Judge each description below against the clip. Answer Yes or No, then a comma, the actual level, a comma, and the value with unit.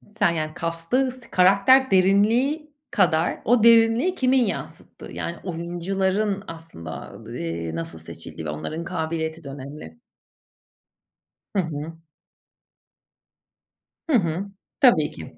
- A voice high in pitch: No, medium, 175 Hz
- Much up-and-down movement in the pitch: Yes, wide, 6.2 semitones